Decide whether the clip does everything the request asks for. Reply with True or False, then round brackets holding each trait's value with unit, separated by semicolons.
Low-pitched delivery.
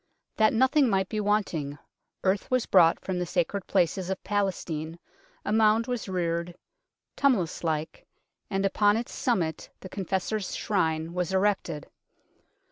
False (190 Hz)